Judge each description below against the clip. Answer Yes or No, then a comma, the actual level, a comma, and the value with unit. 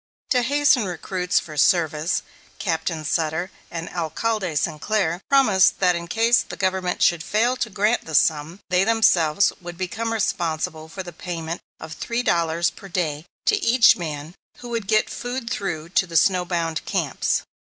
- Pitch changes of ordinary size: Yes, average, 4.9 semitones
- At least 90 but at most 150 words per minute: No, average, 165 wpm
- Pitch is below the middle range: No, medium, 180 Hz